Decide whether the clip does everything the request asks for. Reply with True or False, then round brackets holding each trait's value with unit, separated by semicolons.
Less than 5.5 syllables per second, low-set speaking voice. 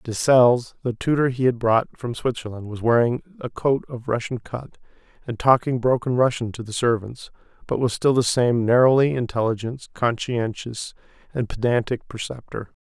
True (5.0 syllables/s; 120 Hz)